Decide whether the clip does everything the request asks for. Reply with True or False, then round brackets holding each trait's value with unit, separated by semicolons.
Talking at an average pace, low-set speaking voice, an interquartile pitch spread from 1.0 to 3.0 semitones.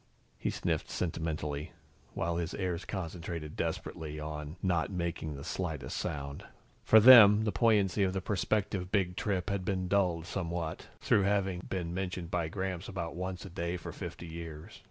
True (160 wpm; 90 Hz; 2.7 semitones)